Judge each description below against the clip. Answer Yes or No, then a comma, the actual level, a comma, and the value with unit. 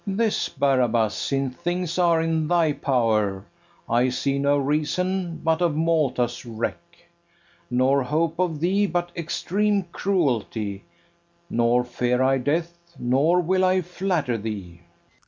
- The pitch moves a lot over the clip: Yes, wide, 6.0 semitones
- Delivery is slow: Yes, slow, 125 wpm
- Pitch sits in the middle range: Yes, medium, 150 Hz